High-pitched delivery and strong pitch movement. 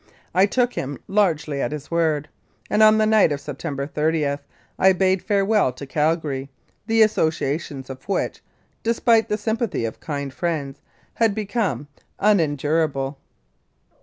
No: medium, 160 Hz; wide, 6.6 semitones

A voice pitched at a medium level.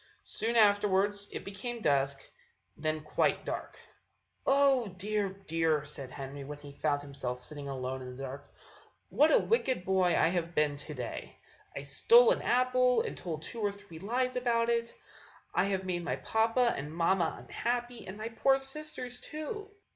No: high, 195 Hz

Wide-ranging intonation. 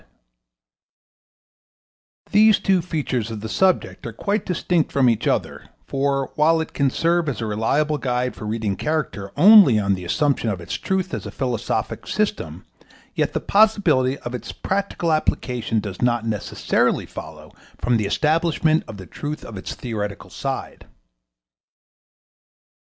Yes: wide, 6.6 semitones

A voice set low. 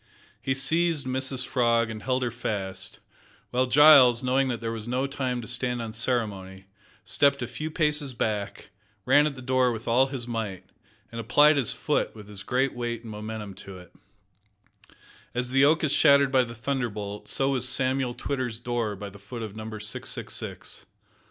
Yes: low, 125 Hz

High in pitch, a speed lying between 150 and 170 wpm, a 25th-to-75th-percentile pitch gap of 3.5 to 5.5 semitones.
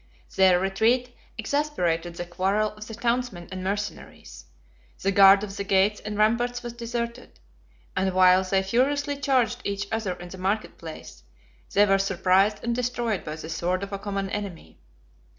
Yes: high, 200 Hz; average, 165 wpm; average, 3.9 semitones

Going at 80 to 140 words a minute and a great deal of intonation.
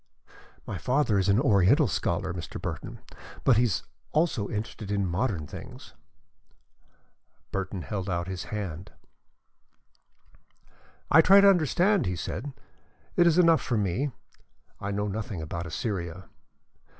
Yes: slow, 135 wpm; wide, 7.2 semitones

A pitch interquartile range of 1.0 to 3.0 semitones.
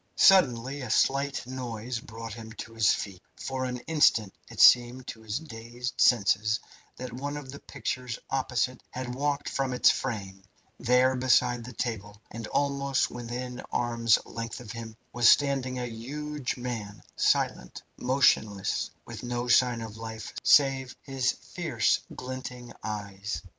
Yes: narrow, 2.6 semitones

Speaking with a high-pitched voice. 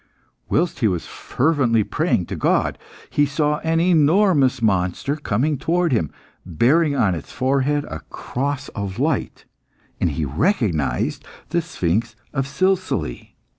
No: low, 135 Hz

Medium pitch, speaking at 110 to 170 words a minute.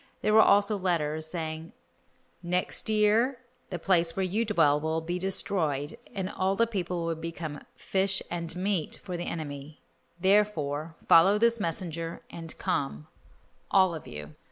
Yes: medium, 175 Hz; average, 150 wpm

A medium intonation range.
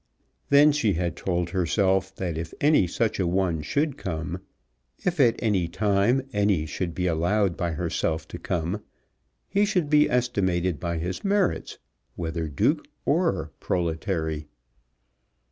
Yes: average, 4.9 semitones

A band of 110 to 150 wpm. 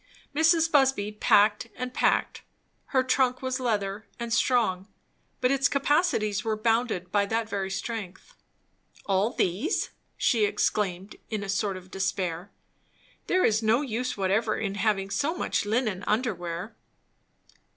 Yes: average, 140 wpm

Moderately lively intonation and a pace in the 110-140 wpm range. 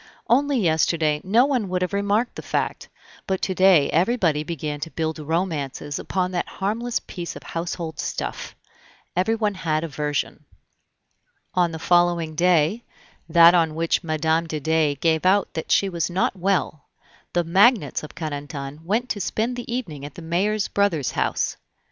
No: average, 3.9 semitones; average, 160 wpm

